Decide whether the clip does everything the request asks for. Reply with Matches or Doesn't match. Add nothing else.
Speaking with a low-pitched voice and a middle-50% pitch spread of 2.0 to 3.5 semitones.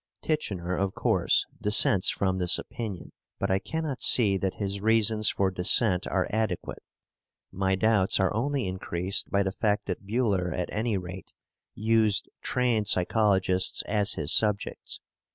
Matches